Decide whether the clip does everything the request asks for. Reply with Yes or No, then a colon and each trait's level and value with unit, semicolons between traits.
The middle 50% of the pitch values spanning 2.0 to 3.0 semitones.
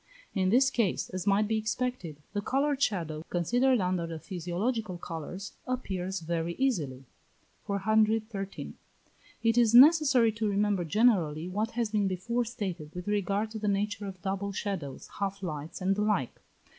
No: average, 3.9 semitones